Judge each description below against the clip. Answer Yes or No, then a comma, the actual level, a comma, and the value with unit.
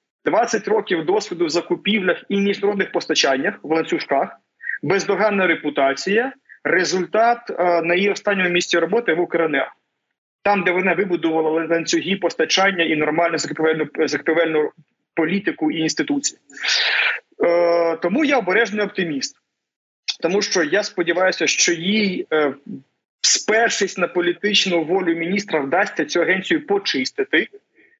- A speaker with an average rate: Yes, average, 120 wpm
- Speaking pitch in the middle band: Yes, medium, 180 Hz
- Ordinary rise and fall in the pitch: Yes, average, 3.9 semitones